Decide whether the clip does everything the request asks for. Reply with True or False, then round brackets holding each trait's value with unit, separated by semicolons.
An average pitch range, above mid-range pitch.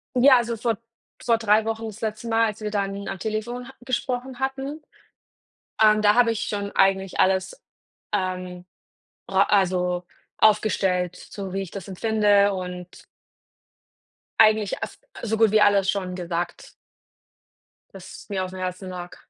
True (3.1 semitones; 205 Hz)